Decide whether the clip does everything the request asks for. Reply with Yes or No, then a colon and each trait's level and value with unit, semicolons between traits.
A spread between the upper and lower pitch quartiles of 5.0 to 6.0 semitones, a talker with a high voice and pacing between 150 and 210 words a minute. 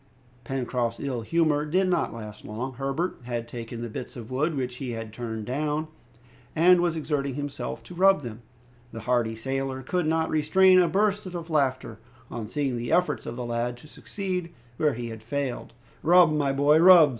No: average, 5.3 semitones; medium, 140 Hz; average, 185 wpm